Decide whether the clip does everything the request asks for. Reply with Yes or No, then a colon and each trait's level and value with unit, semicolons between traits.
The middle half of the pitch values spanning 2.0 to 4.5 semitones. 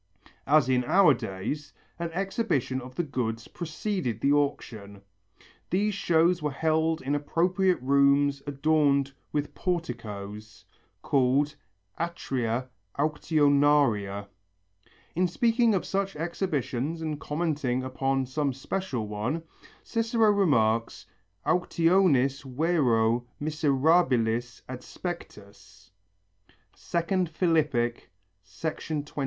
No: average, 5.2 semitones